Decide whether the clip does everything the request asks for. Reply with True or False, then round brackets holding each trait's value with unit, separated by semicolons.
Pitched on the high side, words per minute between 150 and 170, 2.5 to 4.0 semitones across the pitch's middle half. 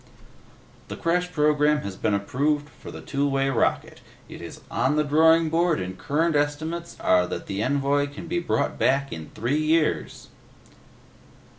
False (145 Hz; 160 wpm; 2.9 semitones)